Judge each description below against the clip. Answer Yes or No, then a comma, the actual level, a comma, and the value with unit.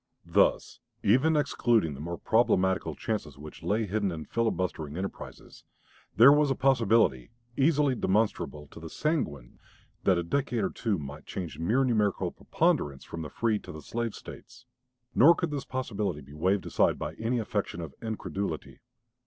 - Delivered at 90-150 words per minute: No, average, 160 wpm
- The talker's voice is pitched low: Yes, low, 105 Hz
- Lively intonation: Yes, wide, 6.7 semitones